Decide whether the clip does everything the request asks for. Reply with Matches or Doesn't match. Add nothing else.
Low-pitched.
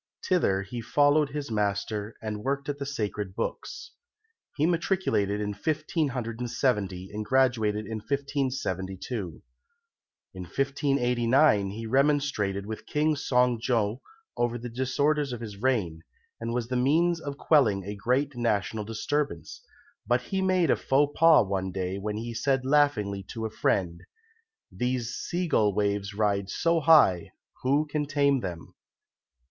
Matches